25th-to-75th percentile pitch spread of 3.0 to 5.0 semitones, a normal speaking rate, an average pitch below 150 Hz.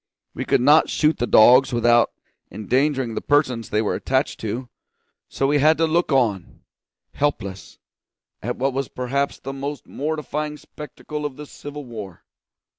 Yes: average, 3.7 semitones; average, 155 wpm; low, 135 Hz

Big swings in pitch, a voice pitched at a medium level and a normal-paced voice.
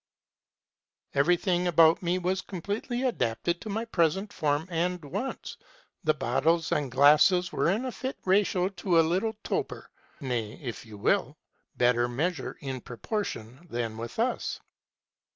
Yes: wide, 6.2 semitones; medium, 170 Hz; average, 150 wpm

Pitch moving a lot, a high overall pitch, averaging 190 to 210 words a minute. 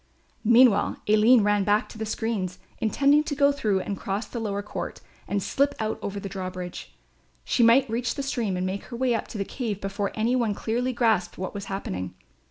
No: average, 3.4 semitones; high, 215 Hz; fast, 205 wpm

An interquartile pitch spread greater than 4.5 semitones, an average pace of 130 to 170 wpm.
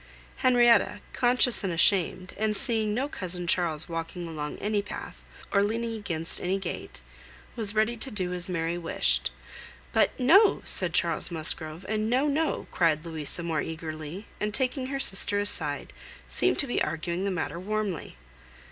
Yes: average, 5.1 semitones; average, 155 wpm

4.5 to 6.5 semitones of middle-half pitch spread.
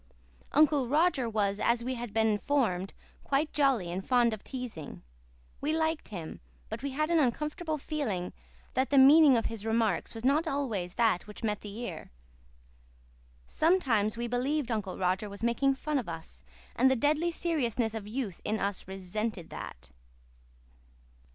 Yes: wide, 5.4 semitones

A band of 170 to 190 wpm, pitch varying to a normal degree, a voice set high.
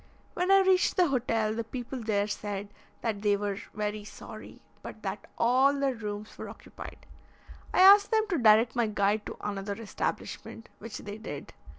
Yes: average, 175 wpm; average, 4.3 semitones; high, 220 Hz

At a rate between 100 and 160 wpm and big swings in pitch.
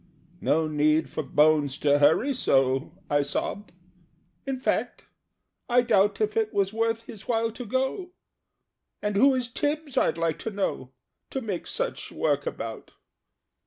Yes: average, 150 wpm; wide, 8.2 semitones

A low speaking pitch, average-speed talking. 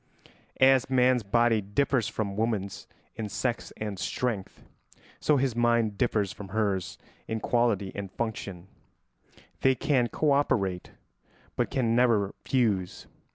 No: low, 110 Hz; slow, 125 wpm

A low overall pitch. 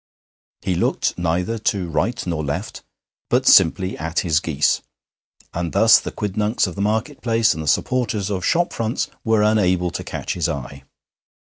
Yes: very low, 95 Hz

